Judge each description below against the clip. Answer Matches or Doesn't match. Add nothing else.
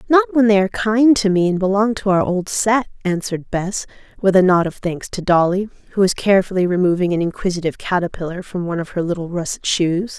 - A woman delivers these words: Matches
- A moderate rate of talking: Doesn't match